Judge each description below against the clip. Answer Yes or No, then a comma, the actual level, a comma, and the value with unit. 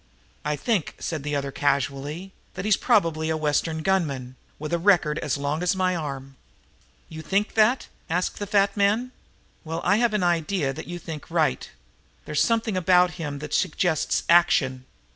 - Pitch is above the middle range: No, medium, 165 Hz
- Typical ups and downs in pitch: Yes, average, 4.5 semitones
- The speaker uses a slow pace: No, average, 165 wpm